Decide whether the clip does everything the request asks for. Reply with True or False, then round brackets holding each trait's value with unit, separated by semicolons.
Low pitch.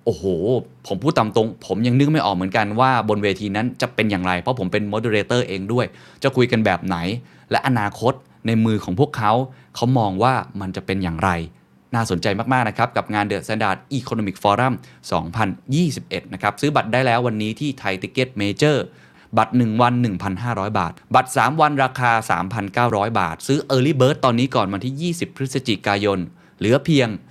True (115 Hz)